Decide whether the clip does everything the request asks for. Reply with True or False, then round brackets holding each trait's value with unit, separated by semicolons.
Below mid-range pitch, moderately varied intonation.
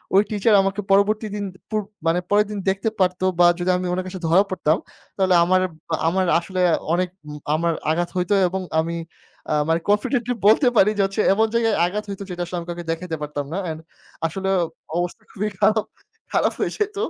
False (185 Hz; 3.1 semitones)